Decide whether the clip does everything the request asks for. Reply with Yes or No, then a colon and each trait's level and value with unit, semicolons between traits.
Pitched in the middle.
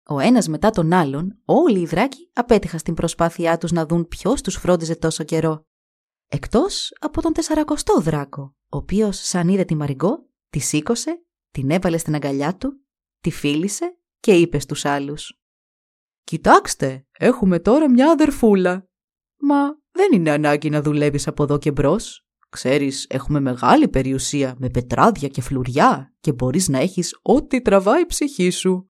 Yes: medium, 170 Hz